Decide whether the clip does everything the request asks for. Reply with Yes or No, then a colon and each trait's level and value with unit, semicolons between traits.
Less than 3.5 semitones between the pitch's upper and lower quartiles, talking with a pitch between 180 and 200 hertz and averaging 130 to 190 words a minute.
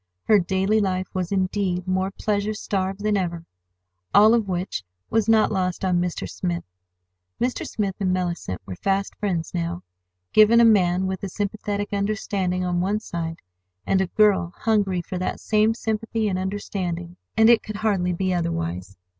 Yes: average, 2.9 semitones; high, 190 Hz; average, 165 wpm